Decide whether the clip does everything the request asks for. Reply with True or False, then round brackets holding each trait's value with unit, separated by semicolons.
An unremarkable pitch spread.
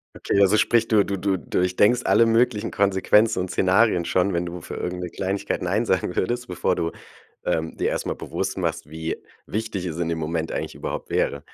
True (3.7 semitones)